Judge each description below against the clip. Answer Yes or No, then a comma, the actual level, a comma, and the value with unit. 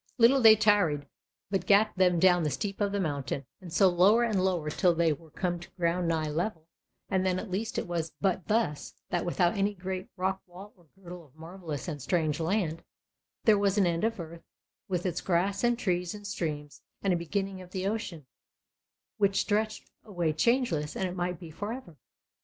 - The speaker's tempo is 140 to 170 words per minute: No, average, 200 wpm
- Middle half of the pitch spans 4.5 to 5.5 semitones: No, average, 3.2 semitones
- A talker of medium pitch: Yes, medium, 180 Hz